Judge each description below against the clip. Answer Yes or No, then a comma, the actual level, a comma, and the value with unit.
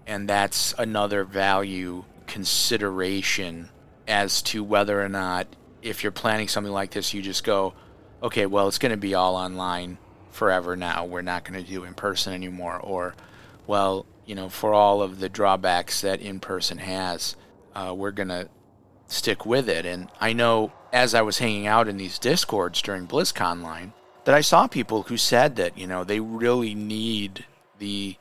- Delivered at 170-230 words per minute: Yes, average, 180 wpm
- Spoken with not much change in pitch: Yes, narrow, 2.3 semitones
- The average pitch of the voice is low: Yes, low, 100 Hz